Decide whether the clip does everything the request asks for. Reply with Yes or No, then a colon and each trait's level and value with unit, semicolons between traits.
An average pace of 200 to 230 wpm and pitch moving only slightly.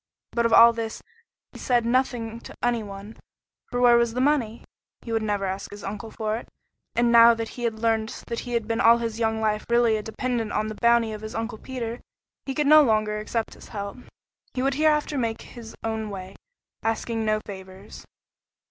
Yes: fast, 205 wpm; narrow, 1.6 semitones